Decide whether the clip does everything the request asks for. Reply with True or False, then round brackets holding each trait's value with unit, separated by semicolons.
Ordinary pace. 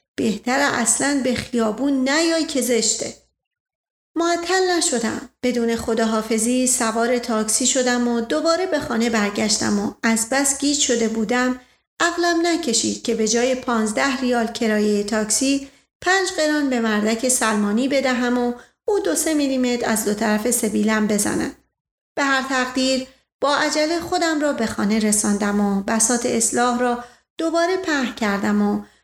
True (140 wpm)